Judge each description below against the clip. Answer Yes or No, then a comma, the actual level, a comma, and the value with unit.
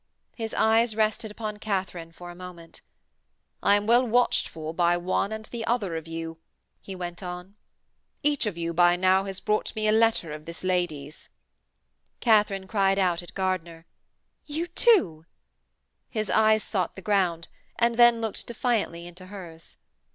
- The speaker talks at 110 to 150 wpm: No, average, 160 wpm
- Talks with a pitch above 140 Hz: Yes, high, 190 Hz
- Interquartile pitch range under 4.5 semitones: Yes, average, 4.1 semitones